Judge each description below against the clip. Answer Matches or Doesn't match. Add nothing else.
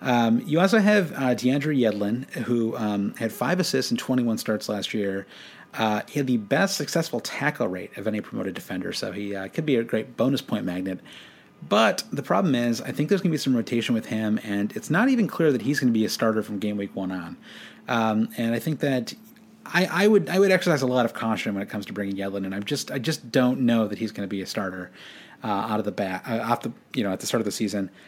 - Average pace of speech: Doesn't match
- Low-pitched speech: Matches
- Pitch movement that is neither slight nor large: Doesn't match